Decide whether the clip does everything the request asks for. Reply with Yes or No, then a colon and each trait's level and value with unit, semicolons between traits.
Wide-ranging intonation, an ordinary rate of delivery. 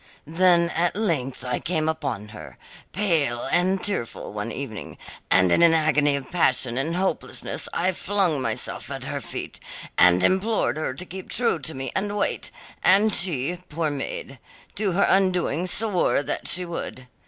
Yes: wide, 5.8 semitones; average, 165 wpm